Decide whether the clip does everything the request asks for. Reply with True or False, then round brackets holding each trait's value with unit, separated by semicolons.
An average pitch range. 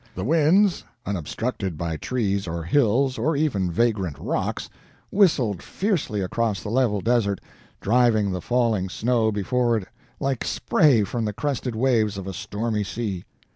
True (4.4 semitones)